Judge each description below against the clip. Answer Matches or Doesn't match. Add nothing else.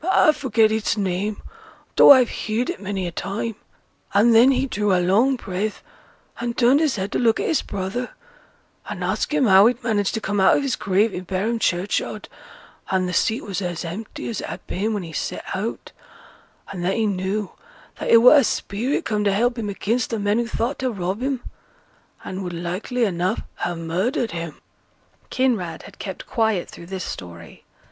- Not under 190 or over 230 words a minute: Matches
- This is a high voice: Matches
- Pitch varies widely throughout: Doesn't match